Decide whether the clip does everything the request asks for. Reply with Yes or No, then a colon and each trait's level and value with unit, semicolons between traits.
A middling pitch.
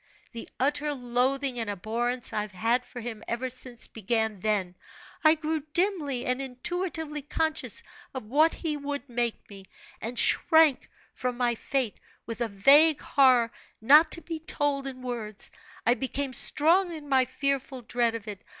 No: very high, 255 Hz